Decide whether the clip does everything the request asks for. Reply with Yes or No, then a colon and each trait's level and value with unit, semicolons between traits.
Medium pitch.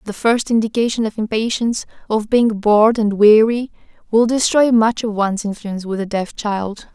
No: high, 220 Hz